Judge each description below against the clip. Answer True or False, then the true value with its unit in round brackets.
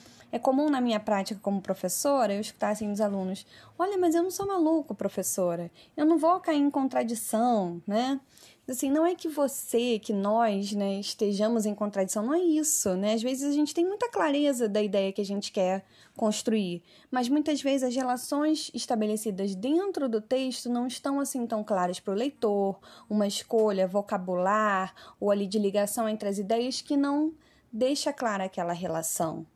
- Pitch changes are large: True (5.8 semitones)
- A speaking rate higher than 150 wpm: True (180 wpm)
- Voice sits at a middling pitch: False (225 Hz)